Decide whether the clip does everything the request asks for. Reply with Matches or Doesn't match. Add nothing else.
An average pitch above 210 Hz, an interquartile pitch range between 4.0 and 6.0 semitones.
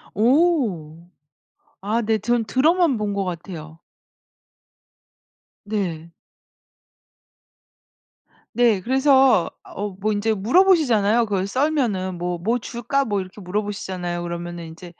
Doesn't match